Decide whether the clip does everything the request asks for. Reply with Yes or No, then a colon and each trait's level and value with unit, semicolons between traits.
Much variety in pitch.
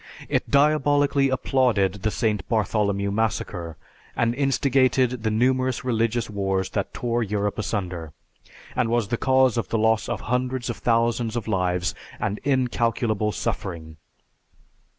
No: average, 3.9 semitones